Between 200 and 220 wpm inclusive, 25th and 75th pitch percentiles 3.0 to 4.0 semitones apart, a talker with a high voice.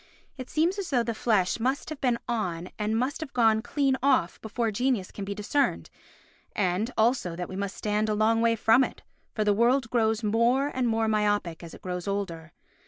Yes: fast, 205 wpm; average, 3.7 semitones; high, 225 Hz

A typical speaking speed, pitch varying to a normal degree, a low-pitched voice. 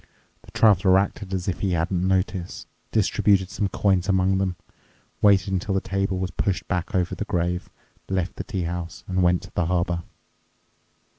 No: average, 170 wpm; narrow, 1.5 semitones; very low, 95 Hz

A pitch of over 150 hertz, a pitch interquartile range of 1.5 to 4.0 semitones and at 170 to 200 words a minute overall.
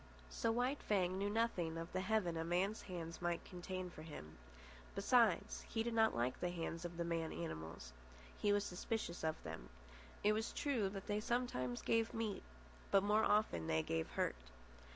No: medium, 185 Hz; average, 4.7 semitones; average, 180 wpm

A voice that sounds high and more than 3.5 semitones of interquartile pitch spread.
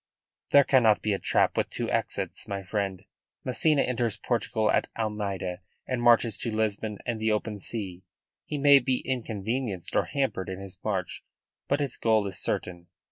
No: low, 110 Hz; average, 4.0 semitones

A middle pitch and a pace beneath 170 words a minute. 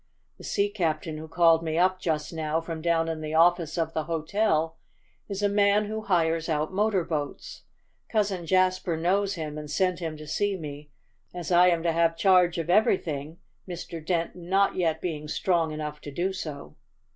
No: medium, 165 Hz; average, 185 wpm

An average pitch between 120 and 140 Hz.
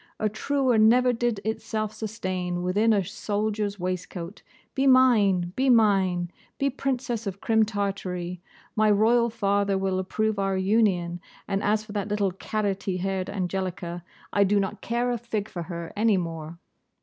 No: high, 205 Hz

